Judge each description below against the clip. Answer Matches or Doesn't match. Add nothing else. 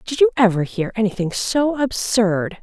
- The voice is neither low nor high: Doesn't match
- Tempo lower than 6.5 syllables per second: Matches